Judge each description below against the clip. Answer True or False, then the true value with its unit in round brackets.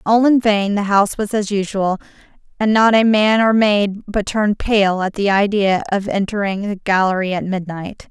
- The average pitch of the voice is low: False (205 Hz)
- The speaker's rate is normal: True (190 wpm)